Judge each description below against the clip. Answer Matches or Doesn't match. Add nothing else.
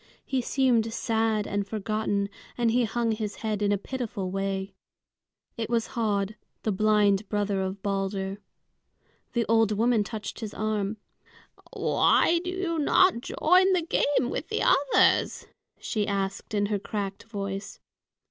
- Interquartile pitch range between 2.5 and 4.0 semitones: Matches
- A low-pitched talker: Doesn't match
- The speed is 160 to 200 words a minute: Doesn't match